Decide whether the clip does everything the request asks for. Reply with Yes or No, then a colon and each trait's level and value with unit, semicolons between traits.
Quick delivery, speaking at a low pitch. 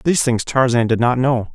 Yes: fast, 235 wpm; low, 125 Hz